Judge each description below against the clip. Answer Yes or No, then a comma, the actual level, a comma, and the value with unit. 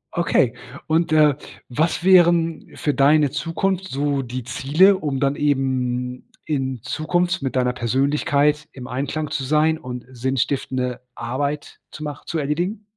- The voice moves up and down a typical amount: Yes, average, 3.3 semitones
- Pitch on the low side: No, medium, 145 Hz